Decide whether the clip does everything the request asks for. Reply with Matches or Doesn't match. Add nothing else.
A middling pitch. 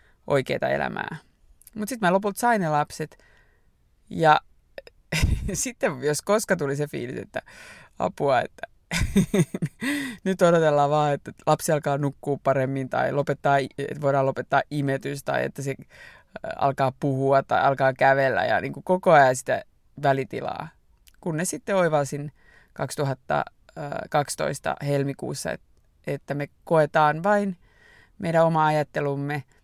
Matches